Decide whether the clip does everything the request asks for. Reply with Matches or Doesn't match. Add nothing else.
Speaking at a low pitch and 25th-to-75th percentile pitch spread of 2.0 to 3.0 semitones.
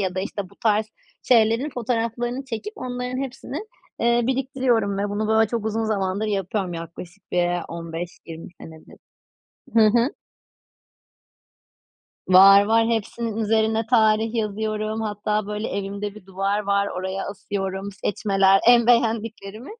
Doesn't match